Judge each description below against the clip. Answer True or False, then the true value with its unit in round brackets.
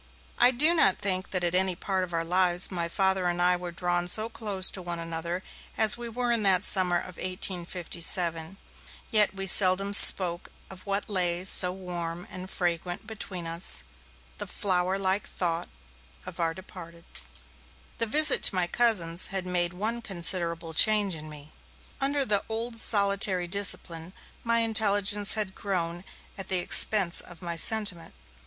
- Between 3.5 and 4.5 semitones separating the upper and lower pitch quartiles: False (2.7 semitones)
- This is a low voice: False (185 Hz)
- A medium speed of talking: True (160 wpm)